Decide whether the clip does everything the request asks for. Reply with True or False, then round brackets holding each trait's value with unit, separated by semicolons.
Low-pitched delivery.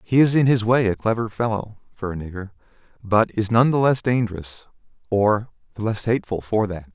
True (110 Hz)